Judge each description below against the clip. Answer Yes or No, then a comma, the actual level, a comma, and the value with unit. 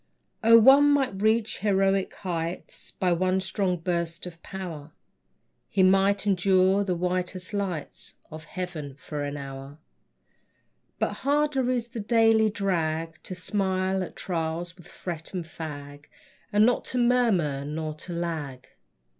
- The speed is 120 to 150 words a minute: Yes, average, 140 wpm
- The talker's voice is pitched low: No, medium, 185 Hz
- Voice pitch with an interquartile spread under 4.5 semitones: Yes, average, 3.9 semitones